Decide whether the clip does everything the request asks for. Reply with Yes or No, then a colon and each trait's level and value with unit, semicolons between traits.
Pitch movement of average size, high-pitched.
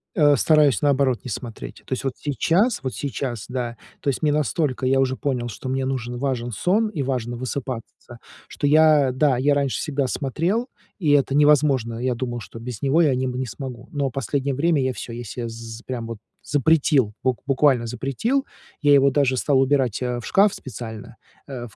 No: average, 3.1 semitones; low, 130 Hz